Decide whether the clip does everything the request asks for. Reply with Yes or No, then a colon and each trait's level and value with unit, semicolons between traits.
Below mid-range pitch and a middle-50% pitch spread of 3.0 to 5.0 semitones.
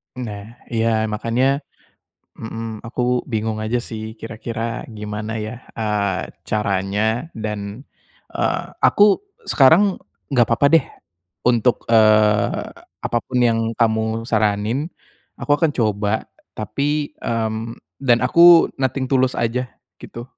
No: low, 115 Hz; narrow, 2.6 semitones